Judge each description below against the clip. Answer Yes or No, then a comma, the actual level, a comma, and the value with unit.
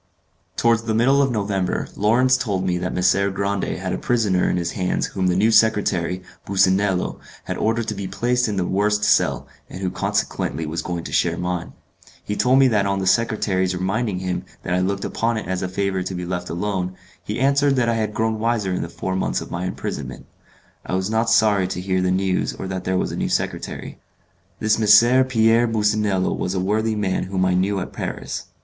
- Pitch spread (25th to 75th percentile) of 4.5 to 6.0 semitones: No, average, 3.3 semitones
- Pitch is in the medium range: No, low, 100 Hz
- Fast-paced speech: Yes, fast, 215 wpm